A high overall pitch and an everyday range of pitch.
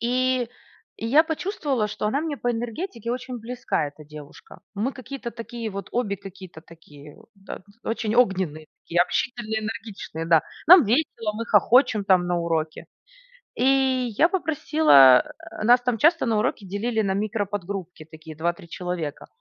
No: high, 220 Hz; wide, 5.8 semitones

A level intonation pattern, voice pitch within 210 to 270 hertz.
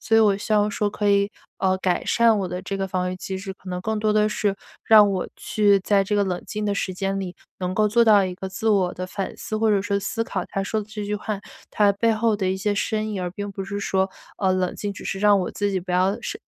No: narrow, 1.9 semitones; high, 200 Hz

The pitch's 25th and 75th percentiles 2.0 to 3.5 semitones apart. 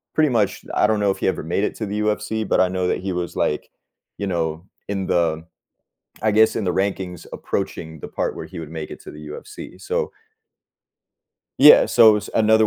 No: average, 4.1 semitones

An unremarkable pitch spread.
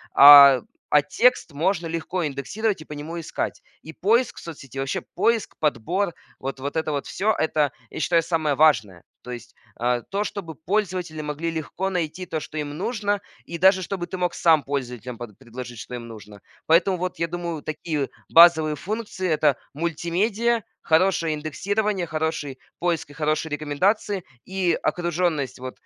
Yes: average, 4.2 semitones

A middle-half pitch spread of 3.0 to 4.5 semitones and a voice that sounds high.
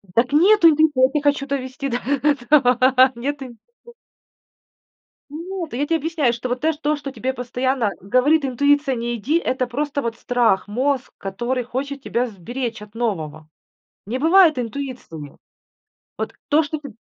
Yes: average, 3.4 semitones; very high, 260 Hz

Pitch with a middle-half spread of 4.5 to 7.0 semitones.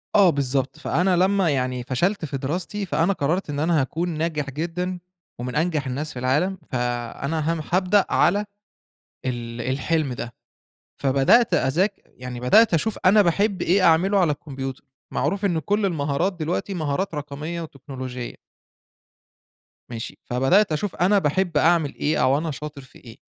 Yes: average, 5.3 semitones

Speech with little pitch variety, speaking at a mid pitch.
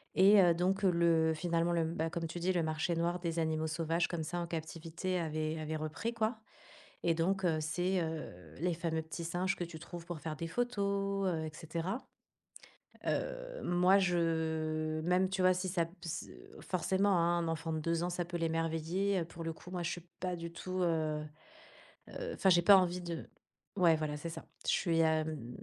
Yes: narrow, 2.1 semitones; medium, 170 Hz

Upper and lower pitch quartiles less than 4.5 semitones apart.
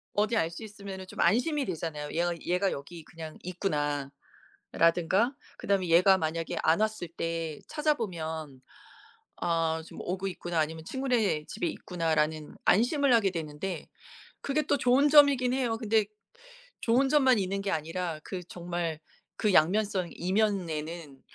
No: average, 5.1 semitones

